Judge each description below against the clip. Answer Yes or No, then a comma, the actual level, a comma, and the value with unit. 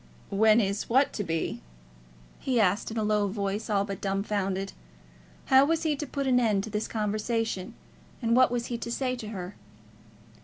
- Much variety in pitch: No, average, 3.4 semitones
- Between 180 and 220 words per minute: Yes, average, 190 wpm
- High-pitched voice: Yes, high, 215 Hz